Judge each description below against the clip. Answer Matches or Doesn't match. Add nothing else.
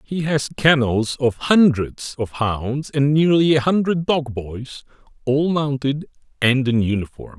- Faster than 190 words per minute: Doesn't match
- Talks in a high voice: Doesn't match